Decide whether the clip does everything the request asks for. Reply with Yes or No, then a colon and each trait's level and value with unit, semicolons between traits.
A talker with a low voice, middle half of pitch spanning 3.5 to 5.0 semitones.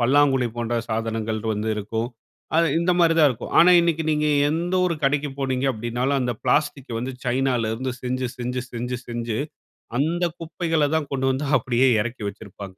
Yes: low, 130 Hz; average, 3.9 semitones